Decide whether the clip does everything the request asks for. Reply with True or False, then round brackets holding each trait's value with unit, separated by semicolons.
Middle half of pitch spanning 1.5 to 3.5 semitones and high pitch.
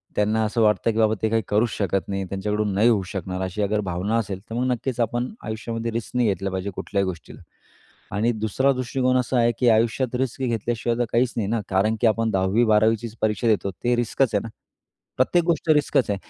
False (2.7 semitones; 110 Hz)